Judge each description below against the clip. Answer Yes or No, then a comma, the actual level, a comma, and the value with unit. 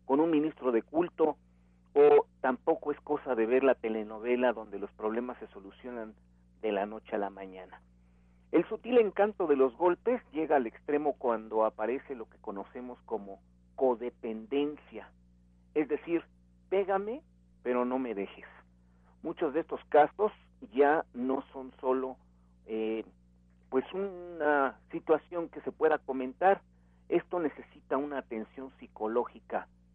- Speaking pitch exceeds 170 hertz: No, low, 125 Hz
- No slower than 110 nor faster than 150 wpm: Yes, average, 135 wpm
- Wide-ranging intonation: Yes, wide, 8.4 semitones